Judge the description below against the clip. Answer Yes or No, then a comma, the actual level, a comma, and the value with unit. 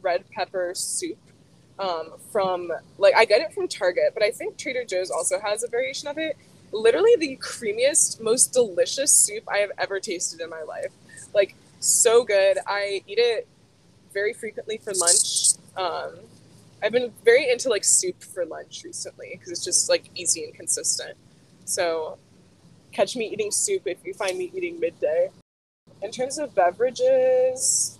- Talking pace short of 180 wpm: Yes, average, 165 wpm